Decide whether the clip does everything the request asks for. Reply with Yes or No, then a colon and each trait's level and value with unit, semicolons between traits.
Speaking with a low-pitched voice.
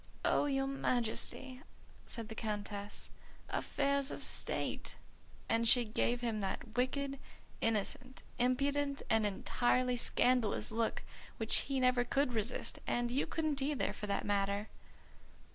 No: high, 245 Hz